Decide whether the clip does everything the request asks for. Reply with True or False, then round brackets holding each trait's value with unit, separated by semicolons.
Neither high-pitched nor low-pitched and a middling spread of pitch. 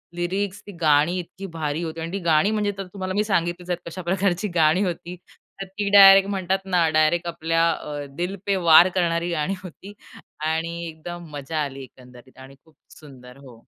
True (170 Hz; 3.5 semitones)